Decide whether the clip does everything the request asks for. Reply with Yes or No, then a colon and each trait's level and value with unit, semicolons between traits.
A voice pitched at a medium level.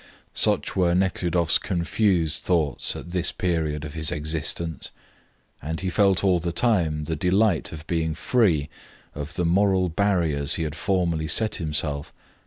No: very low, 85 Hz